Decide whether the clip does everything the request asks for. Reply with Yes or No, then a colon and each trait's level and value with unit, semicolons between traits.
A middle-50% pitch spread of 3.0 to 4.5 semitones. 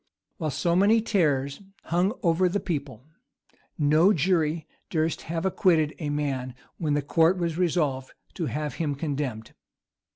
Yes: average, 3.4 semitones